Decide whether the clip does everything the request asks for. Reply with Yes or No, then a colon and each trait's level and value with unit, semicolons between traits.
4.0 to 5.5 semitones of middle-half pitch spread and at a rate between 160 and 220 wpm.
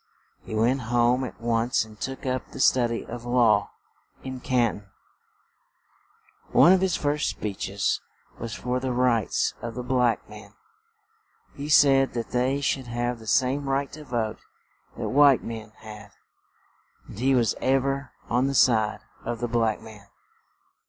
No: average, 2.8 semitones; average, 165 wpm